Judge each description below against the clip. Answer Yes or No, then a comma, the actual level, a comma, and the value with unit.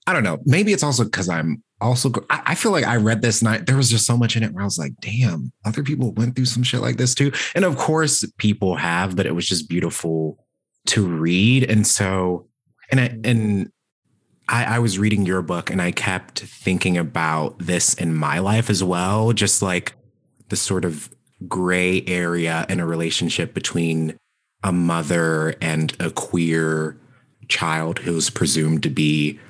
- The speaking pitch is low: Yes, very low, 95 Hz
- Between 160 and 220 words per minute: Yes, average, 185 wpm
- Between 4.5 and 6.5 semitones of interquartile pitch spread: Yes, wide, 5.6 semitones